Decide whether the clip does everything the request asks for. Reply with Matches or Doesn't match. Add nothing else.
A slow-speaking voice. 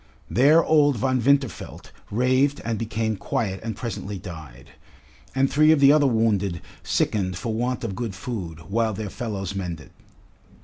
Doesn't match